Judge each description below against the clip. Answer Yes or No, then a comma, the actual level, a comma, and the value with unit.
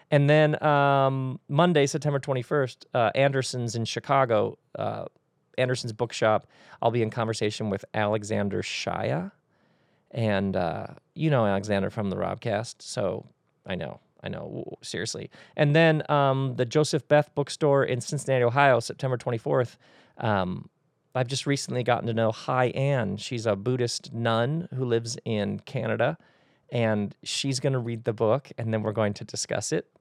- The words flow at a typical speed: Yes, average, 155 wpm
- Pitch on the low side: Yes, low, 125 Hz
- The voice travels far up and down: No, average, 4.0 semitones